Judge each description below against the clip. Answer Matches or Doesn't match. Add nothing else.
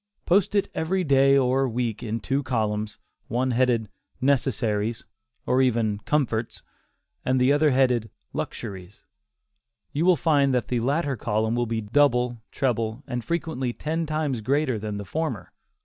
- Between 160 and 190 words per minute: Doesn't match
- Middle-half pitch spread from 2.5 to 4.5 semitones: Matches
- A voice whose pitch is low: Matches